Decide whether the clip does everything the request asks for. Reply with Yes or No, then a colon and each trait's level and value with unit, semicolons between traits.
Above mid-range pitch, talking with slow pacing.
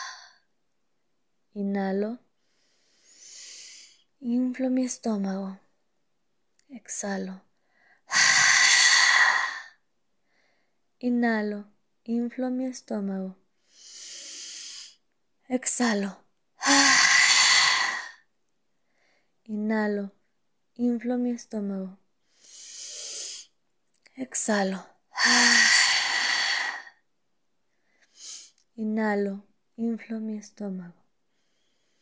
Yes: high, 235 Hz; slow, 35 wpm